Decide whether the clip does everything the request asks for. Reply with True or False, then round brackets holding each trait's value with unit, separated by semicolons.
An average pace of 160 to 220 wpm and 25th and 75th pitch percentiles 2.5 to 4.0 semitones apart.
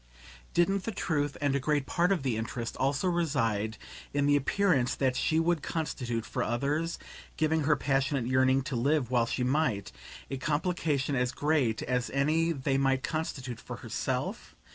True (165 wpm; 3.7 semitones)